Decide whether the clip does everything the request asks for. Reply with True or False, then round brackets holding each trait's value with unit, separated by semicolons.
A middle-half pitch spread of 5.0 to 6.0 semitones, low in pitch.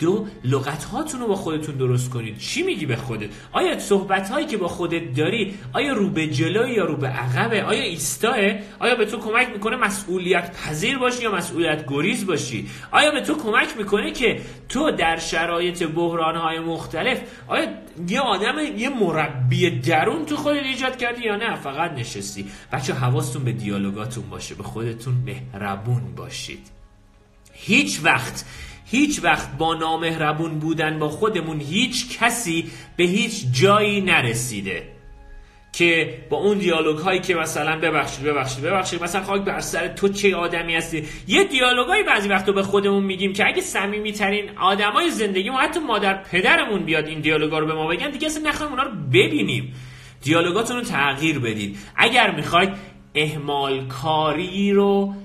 False (5.4 semitones; 170 Hz)